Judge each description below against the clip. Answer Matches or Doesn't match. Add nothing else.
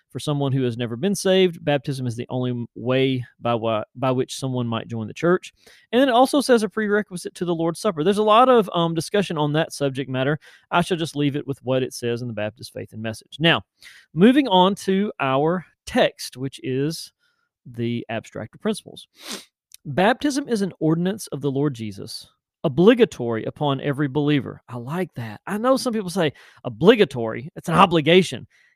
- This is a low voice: Doesn't match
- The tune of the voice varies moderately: Doesn't match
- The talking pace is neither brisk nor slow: Matches